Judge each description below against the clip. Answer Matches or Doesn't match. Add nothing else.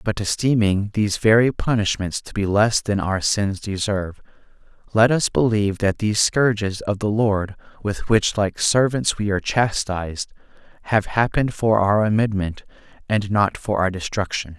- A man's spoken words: Matches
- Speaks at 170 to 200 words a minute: Doesn't match